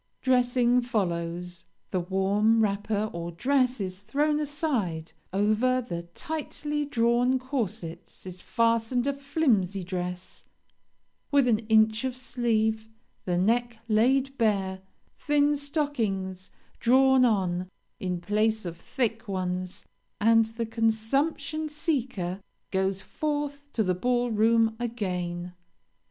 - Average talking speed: No, slow, 115 wpm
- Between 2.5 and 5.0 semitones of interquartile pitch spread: No, wide, 5.4 semitones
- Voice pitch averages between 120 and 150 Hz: No, high, 225 Hz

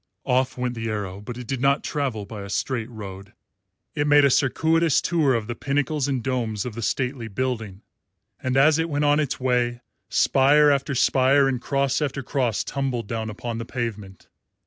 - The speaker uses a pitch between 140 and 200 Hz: No, low, 130 Hz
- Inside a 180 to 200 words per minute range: Yes, average, 190 wpm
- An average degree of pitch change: Yes, average, 3.5 semitones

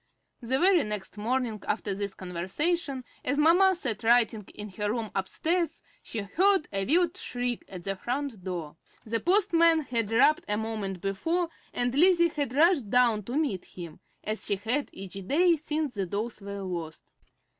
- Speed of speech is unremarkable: Yes, average, 165 wpm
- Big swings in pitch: Yes, wide, 7.6 semitones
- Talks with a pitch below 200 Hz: No, high, 235 Hz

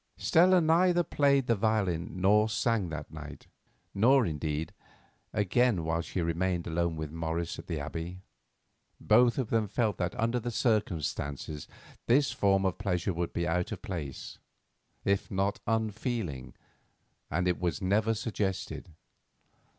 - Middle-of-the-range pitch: No, very low, 95 Hz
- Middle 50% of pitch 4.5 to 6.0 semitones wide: Yes, average, 5.1 semitones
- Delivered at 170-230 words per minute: No, average, 140 wpm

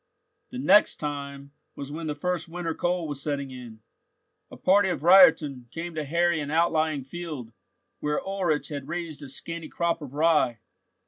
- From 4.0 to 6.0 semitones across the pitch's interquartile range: No, average, 3.5 semitones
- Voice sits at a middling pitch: Yes, medium, 155 Hz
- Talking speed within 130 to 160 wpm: No, average, 170 wpm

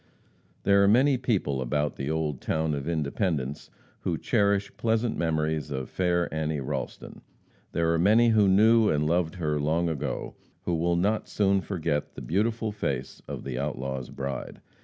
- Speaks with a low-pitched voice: Yes, very low, 85 Hz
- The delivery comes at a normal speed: Yes, average, 160 wpm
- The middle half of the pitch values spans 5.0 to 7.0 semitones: Yes, wide, 5.4 semitones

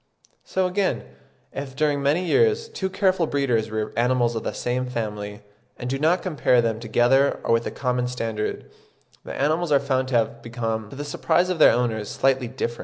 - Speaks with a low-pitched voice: Yes, low, 130 Hz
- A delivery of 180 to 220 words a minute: Yes, average, 190 wpm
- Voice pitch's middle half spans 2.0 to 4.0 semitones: No, average, 4.5 semitones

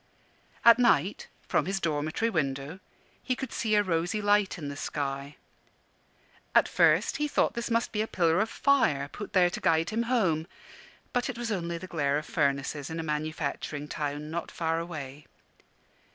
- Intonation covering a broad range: Yes, wide, 6.3 semitones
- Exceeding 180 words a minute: No, average, 175 wpm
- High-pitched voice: No, medium, 165 Hz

